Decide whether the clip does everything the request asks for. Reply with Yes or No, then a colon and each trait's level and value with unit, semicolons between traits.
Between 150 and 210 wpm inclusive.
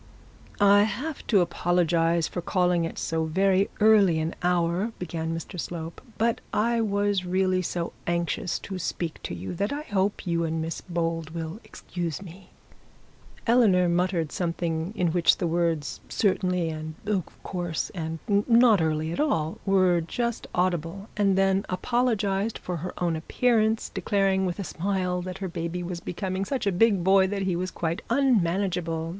Yes: average, 160 wpm